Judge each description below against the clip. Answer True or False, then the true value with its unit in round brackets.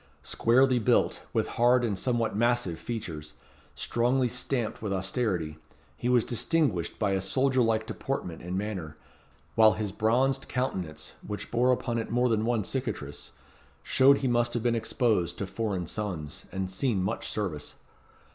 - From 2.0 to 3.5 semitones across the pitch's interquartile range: False (4.5 semitones)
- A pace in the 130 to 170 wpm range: True (155 wpm)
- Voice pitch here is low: True (115 Hz)